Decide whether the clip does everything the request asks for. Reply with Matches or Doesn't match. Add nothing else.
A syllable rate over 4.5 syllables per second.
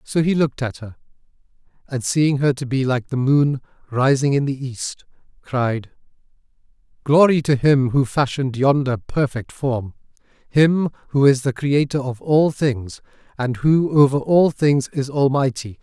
Doesn't match